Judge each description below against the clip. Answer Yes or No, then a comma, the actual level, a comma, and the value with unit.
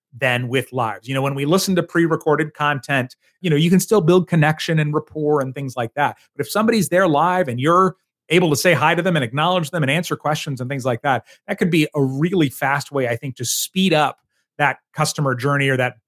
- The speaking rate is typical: No, fast, 245 wpm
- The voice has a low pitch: No, medium, 150 Hz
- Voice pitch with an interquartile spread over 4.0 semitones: Yes, average, 4.4 semitones